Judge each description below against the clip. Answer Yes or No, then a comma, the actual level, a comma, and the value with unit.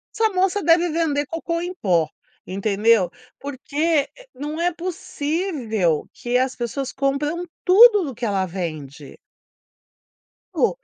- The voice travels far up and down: Yes, wide, 8.0 semitones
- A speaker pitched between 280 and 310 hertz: Yes, very high, 285 Hz